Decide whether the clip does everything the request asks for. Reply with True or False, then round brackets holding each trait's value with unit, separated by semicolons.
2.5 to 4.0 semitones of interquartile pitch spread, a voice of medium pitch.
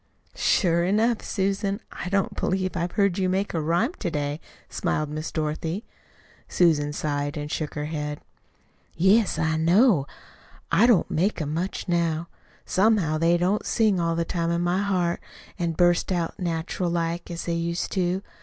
True (3.0 semitones; 170 Hz)